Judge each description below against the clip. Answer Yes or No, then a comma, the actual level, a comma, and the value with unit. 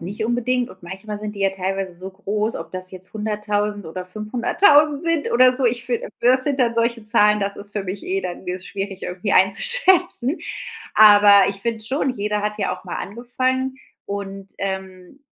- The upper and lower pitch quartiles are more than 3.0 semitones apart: Yes, average, 3.9 semitones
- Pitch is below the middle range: No, high, 210 Hz